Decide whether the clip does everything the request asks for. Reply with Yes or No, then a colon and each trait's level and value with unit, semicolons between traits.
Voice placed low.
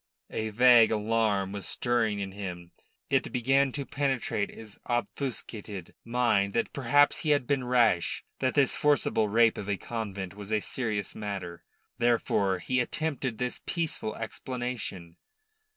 Yes: low, 115 Hz